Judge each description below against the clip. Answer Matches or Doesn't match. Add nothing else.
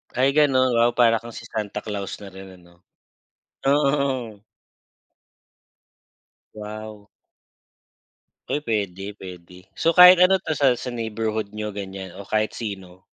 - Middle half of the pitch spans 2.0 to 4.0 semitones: Doesn't match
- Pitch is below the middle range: Matches